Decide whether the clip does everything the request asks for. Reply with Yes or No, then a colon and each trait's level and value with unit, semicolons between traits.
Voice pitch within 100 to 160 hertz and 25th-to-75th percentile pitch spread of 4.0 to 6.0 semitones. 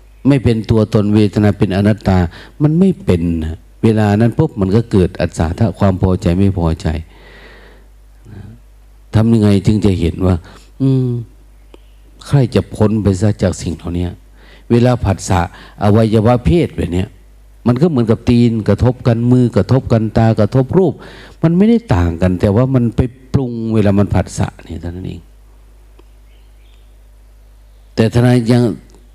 Yes: low, 110 Hz; average, 4.4 semitones